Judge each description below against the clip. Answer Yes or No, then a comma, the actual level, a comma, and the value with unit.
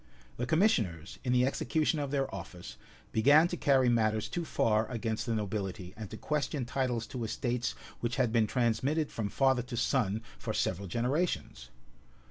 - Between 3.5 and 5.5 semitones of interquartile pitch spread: Yes, average, 3.9 semitones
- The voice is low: Yes, low, 120 Hz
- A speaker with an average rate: Yes, average, 170 wpm